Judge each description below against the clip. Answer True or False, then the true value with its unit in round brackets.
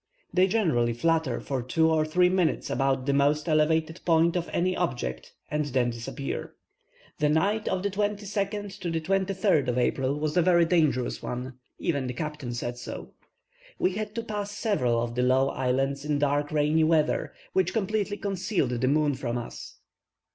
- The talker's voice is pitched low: False (155 Hz)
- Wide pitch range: True (5.8 semitones)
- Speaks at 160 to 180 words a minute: True (175 wpm)